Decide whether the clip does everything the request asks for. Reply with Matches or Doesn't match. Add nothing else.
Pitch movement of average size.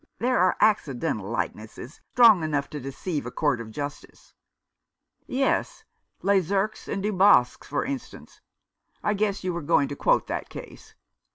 Doesn't match